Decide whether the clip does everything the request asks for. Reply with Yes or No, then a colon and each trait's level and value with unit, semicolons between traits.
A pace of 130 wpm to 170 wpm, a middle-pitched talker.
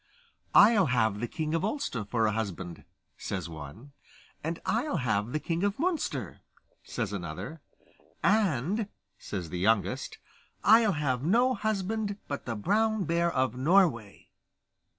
Yes: slow, 135 wpm; medium, 150 Hz